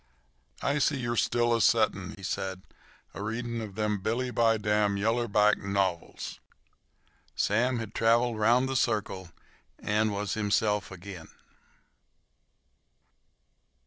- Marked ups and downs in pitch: No, average, 2.8 semitones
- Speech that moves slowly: Yes, slow, 125 wpm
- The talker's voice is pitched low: Yes, low, 110 Hz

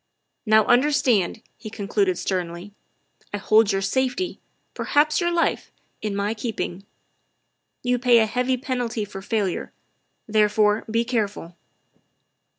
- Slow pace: Yes, slow, 130 wpm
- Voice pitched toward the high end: Yes, high, 220 Hz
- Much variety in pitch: No, average, 3.7 semitones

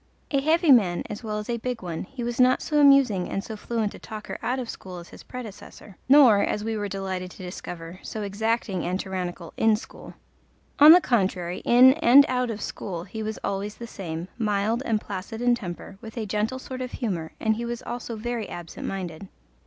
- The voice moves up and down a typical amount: Yes, average, 4.1 semitones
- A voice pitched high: Yes, high, 215 Hz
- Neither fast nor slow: No, fast, 210 wpm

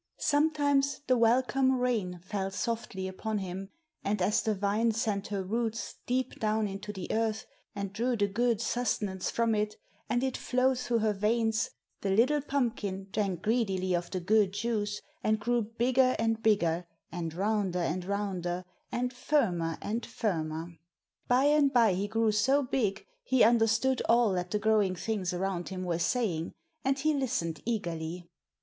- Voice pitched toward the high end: Yes, high, 215 Hz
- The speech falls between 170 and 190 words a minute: No, average, 160 wpm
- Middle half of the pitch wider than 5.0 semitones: No, average, 4.0 semitones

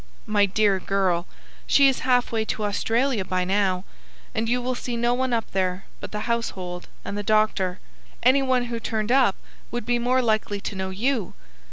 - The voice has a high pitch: Yes, high, 215 Hz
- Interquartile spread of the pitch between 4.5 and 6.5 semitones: No, average, 3.9 semitones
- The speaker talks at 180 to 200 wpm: Yes, average, 190 wpm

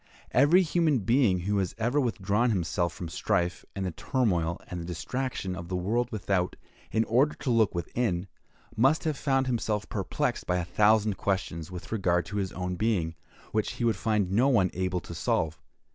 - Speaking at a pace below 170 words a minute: No, average, 190 wpm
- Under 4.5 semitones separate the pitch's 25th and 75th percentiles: No, average, 5.1 semitones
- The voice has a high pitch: No, low, 100 Hz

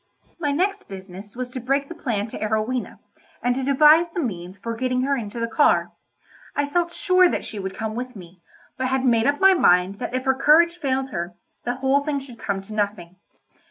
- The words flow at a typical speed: No, fast, 215 wpm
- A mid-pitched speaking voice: No, very high, 255 Hz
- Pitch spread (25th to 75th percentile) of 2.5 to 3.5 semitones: No, wide, 5.4 semitones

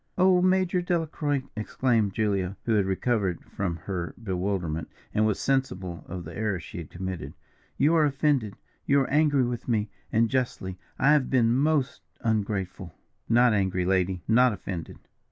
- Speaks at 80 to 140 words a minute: No, average, 155 wpm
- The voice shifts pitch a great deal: Yes, wide, 6.1 semitones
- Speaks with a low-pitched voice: Yes, low, 110 Hz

